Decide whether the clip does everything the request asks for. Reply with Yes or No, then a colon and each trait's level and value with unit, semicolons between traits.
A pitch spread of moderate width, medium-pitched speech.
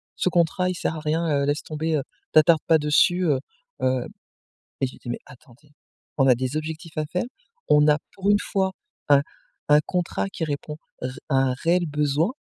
Yes: average, 3.1 semitones; medium, 150 Hz